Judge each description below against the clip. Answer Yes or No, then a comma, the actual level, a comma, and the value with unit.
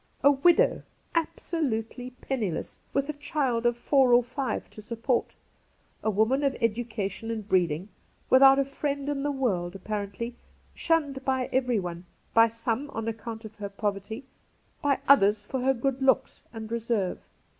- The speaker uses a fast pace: No, average, 155 wpm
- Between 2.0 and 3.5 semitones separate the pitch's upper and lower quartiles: No, average, 3.9 semitones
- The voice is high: Yes, high, 240 Hz